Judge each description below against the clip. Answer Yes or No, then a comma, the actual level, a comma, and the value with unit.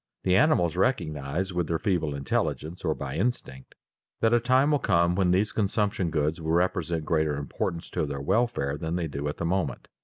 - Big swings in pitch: No, average, 4.2 semitones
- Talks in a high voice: No, very low, 85 Hz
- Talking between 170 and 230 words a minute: Yes, average, 190 wpm